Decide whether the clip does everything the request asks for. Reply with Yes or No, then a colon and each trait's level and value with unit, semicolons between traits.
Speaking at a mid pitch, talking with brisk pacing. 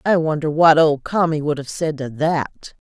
Yes: medium, 155 Hz; fast, 210 wpm